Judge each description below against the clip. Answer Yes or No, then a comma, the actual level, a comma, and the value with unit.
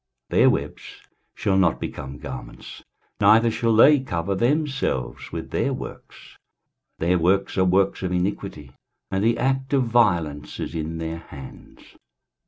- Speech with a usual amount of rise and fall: No, wide, 6.0 semitones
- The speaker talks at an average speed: Yes, average, 145 wpm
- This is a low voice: Yes, very low, 95 Hz